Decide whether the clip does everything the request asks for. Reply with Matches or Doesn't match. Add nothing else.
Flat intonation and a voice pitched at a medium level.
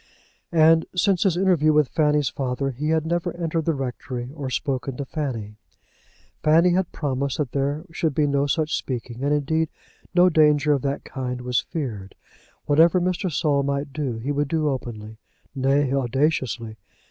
Doesn't match